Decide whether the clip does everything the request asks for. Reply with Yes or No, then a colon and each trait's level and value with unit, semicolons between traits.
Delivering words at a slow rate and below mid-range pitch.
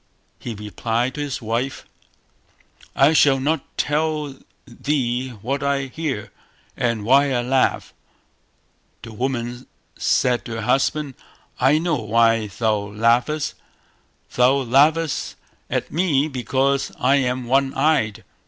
Yes: slow, 120 wpm; low, 130 Hz